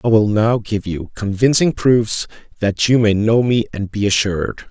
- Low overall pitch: Yes, low, 110 Hz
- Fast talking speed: No, average, 190 wpm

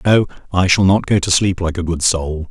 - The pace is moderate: No, fast, 265 wpm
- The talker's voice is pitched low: Yes, very low, 90 Hz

